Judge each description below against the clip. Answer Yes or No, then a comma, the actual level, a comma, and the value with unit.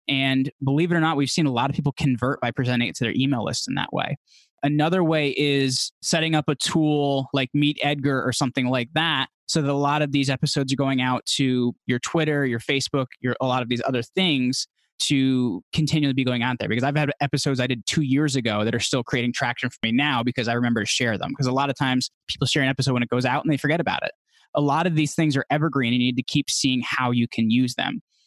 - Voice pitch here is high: No, low, 135 Hz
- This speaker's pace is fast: Yes, fast, 265 wpm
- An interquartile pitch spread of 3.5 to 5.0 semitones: No, average, 2.7 semitones